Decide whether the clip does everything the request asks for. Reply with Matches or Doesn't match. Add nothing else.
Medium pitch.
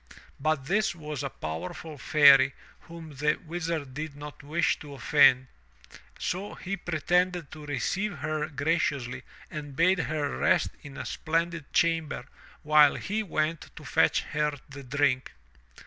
Matches